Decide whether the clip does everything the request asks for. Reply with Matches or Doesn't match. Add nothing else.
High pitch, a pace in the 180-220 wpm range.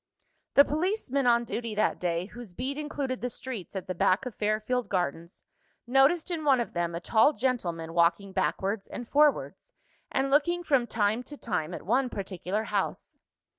Doesn't match